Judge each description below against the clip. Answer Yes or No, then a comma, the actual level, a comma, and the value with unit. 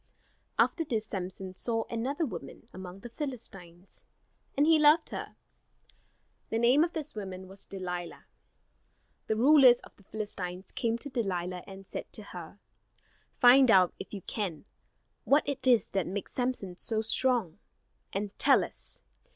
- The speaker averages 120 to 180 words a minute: Yes, average, 150 wpm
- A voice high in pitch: Yes, high, 215 Hz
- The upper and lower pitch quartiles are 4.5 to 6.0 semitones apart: Yes, wide, 5.4 semitones